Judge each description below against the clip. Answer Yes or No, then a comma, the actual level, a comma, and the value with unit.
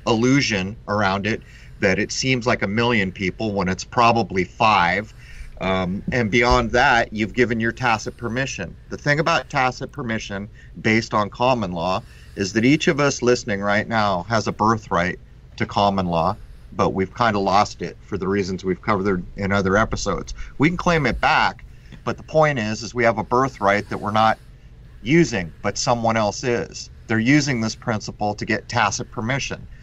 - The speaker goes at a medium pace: Yes, average, 180 wpm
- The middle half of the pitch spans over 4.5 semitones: No, average, 3.5 semitones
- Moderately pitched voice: No, low, 110 Hz